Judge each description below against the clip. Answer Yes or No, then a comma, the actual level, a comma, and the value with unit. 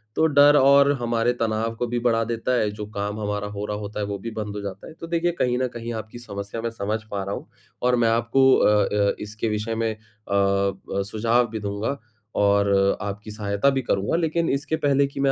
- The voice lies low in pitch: Yes, low, 110 Hz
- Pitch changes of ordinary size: Yes, average, 3.2 semitones